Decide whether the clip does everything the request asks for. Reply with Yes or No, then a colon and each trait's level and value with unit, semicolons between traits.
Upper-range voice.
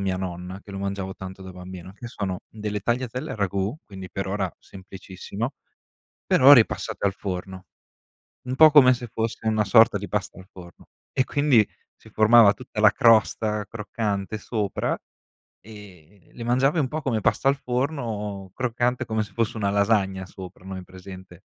No: low, 105 Hz